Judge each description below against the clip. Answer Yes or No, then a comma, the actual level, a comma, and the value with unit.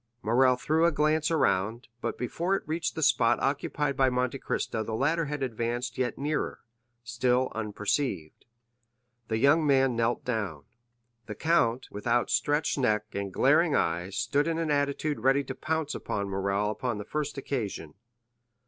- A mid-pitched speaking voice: No, low, 125 Hz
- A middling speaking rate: Yes, average, 155 wpm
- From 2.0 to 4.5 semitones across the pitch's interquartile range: No, average, 4.9 semitones